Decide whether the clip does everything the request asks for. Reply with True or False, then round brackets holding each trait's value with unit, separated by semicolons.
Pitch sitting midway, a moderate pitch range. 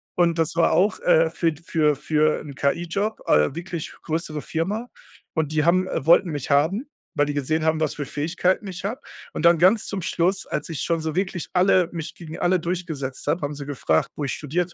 True (165 Hz; 3.3 semitones)